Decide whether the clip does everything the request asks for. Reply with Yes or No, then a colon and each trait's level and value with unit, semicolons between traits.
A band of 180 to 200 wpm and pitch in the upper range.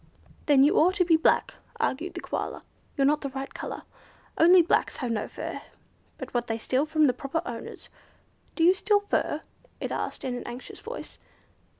Yes: average, 190 wpm; very high, 295 Hz